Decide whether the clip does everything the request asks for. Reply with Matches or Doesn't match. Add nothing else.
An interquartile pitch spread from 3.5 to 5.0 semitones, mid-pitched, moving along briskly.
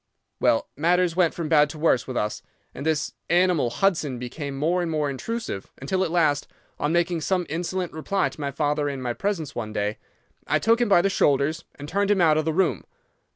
Matches